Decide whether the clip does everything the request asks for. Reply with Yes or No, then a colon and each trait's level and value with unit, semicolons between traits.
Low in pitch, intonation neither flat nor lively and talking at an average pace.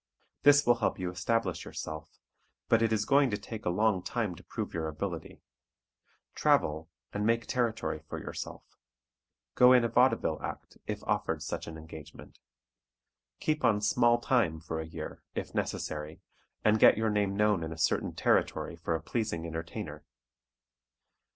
No: low, 105 Hz; wide, 6.0 semitones; average, 160 wpm